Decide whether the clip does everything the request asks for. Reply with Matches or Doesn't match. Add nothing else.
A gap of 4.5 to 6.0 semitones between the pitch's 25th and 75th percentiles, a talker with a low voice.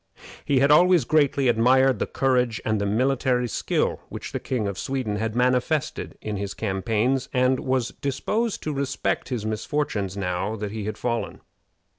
Doesn't match